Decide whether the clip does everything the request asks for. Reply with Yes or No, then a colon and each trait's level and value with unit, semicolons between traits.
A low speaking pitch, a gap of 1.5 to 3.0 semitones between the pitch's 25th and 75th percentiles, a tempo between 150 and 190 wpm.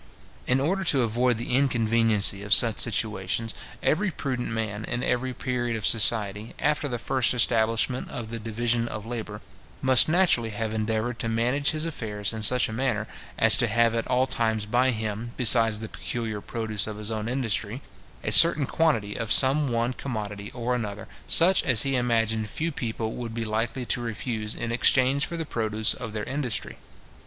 Yes: low, 115 Hz; narrow, 2.6 semitones; average, 180 wpm